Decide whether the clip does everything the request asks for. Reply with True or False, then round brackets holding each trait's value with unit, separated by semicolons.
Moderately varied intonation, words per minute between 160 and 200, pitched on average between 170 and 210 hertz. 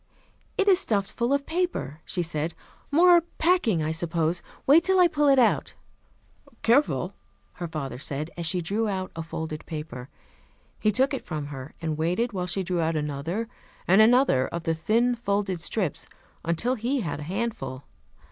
False (7.3 semitones; 175 wpm; 185 Hz)